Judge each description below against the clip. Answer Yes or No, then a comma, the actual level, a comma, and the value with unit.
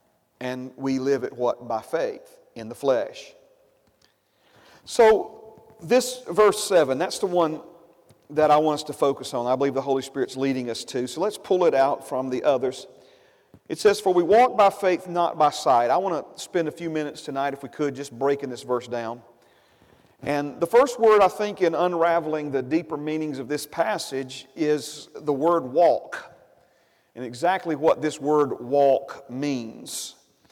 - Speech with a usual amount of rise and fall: No, wide, 5.7 semitones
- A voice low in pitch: No, medium, 150 Hz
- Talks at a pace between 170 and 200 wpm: Yes, average, 180 wpm